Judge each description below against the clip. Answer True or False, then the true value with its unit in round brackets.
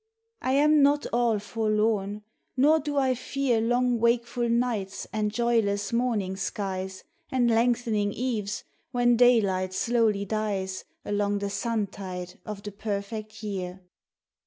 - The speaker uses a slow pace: True (125 wpm)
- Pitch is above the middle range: True (220 Hz)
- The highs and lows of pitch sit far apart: False (3.2 semitones)